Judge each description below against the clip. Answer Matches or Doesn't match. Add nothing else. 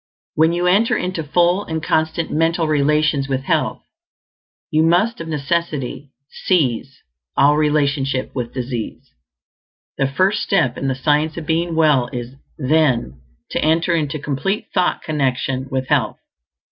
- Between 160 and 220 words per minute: Doesn't match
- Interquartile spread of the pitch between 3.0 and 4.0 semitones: Matches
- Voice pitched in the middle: Matches